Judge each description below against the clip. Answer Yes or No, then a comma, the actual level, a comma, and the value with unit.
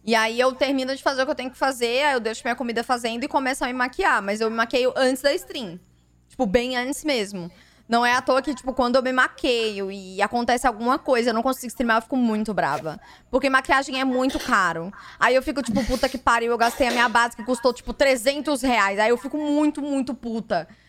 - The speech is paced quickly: Yes, fast, 240 wpm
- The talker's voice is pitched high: Yes, very high, 255 Hz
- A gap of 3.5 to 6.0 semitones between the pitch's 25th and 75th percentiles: No, narrow, 2.6 semitones